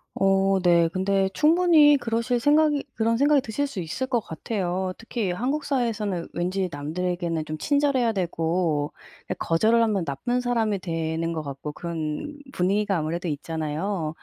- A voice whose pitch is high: Yes, high, 195 Hz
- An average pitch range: No, wide, 6.4 semitones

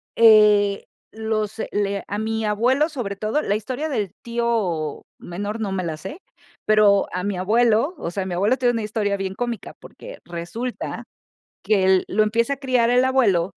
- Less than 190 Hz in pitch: No, high, 215 Hz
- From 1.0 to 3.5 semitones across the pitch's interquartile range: Yes, average, 3.1 semitones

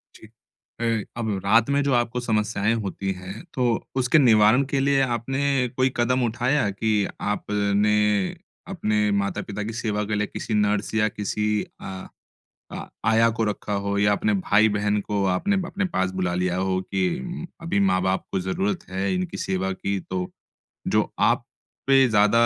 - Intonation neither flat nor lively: Yes, average, 3.2 semitones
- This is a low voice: Yes, low, 105 Hz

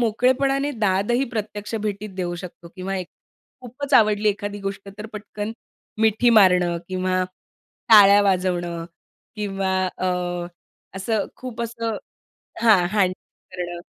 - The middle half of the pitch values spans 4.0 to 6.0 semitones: No, average, 3.1 semitones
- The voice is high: Yes, high, 205 Hz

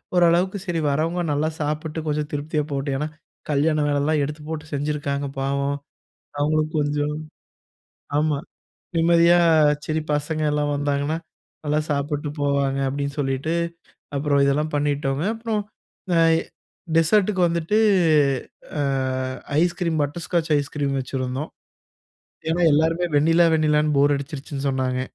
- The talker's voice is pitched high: No, medium, 150 Hz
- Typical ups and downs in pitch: No, narrow, 2.2 semitones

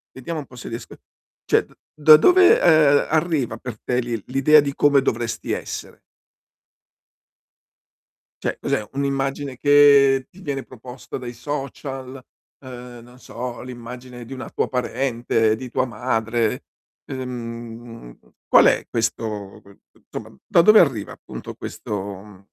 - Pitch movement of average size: Yes, average, 3.1 semitones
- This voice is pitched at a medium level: No, low, 125 Hz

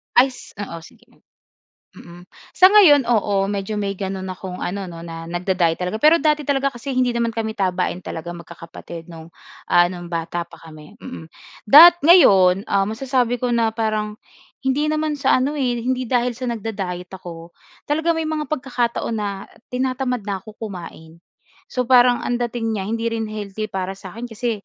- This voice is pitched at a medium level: No, high, 220 Hz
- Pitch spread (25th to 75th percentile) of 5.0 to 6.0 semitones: Yes, wide, 5.5 semitones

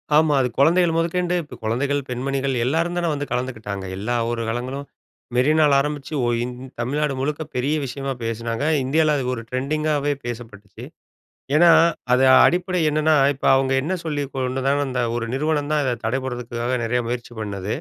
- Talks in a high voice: No, low, 135 Hz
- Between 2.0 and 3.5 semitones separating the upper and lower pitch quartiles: No, average, 3.9 semitones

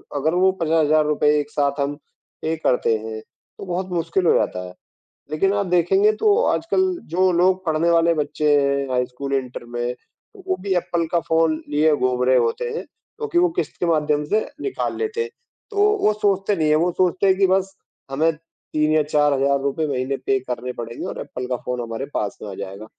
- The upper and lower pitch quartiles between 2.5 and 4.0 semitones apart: No, wide, 5.6 semitones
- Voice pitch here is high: No, medium, 155 Hz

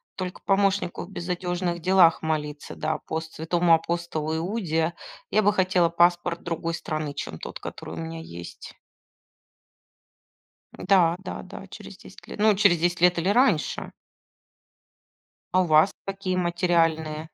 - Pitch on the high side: No, medium, 175 Hz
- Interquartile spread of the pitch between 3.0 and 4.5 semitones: No, narrow, 2.6 semitones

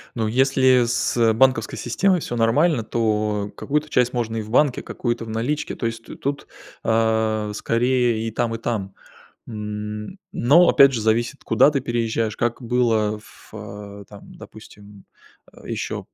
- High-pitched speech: No, low, 115 Hz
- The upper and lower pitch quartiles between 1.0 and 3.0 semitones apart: Yes, narrow, 2.6 semitones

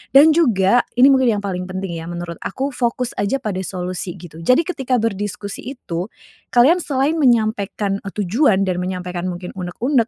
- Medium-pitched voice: No, high, 205 Hz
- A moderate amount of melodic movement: No, wide, 5.8 semitones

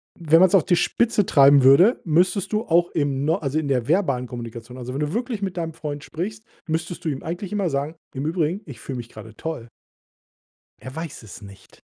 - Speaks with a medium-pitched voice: Yes, medium, 155 Hz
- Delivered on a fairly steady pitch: No, average, 4.9 semitones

